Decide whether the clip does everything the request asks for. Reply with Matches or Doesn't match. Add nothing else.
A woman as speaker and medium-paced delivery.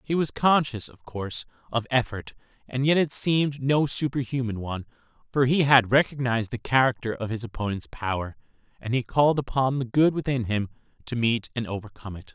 Doesn't match